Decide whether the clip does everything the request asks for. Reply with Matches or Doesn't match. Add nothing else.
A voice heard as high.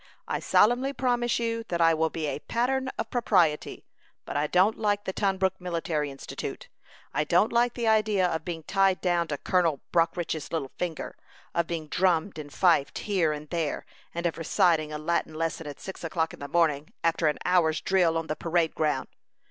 Doesn't match